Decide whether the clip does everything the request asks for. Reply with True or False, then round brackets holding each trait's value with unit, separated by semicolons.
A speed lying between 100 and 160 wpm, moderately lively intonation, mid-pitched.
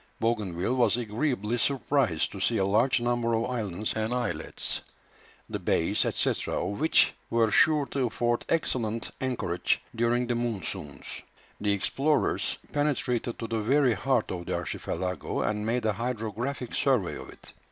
False (150 wpm; 3.1 semitones; 115 Hz)